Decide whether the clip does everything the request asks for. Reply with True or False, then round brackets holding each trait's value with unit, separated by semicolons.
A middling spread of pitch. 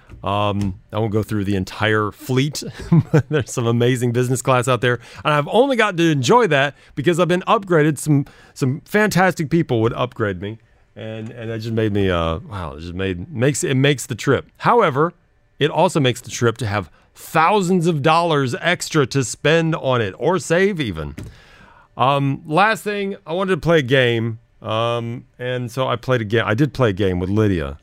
False (6.1 semitones)